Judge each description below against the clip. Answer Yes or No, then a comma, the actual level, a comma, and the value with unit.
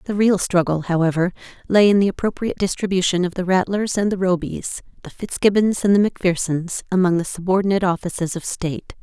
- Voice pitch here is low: No, medium, 185 Hz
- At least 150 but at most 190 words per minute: Yes, average, 175 wpm